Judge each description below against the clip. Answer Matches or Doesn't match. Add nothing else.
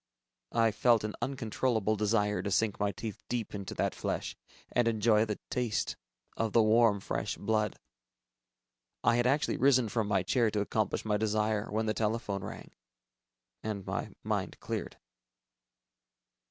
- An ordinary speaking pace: Matches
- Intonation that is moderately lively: Doesn't match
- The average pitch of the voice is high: Doesn't match